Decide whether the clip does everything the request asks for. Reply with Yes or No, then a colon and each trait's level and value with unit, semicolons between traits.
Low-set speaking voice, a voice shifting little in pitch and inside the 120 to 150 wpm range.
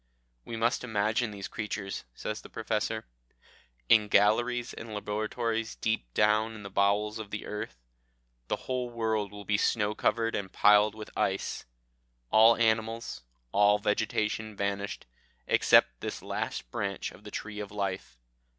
Yes: low, 105 Hz; narrow, 1.5 semitones; average, 145 wpm